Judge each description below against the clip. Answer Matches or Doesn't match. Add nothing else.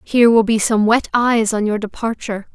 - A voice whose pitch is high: Matches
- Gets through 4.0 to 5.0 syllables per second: Doesn't match